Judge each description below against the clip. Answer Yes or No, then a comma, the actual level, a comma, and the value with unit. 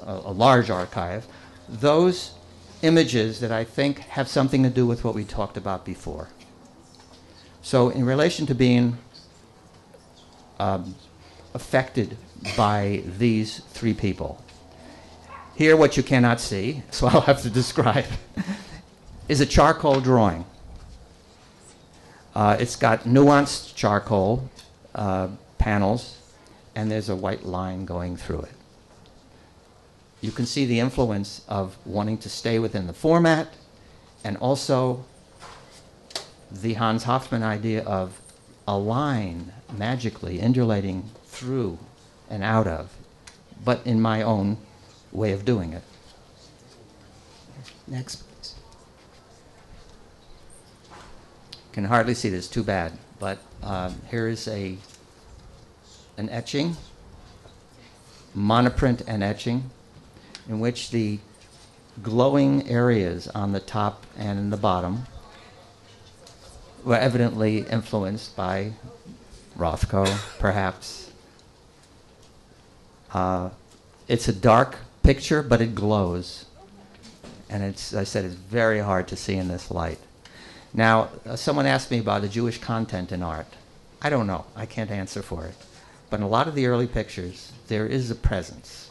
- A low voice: Yes, low, 110 Hz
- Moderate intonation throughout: Yes, average, 4.3 semitones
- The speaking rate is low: Yes, slow, 120 wpm